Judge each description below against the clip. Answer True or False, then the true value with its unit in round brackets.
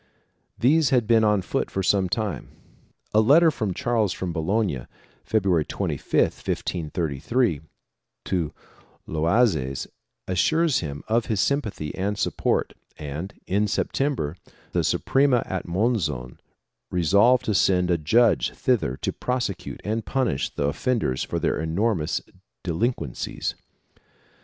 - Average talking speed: False (125 wpm)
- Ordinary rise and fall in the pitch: False (6.4 semitones)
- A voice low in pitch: True (100 Hz)